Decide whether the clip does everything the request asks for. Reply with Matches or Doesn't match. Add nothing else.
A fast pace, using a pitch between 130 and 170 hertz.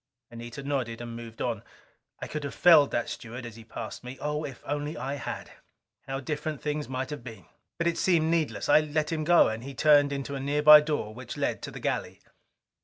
Matches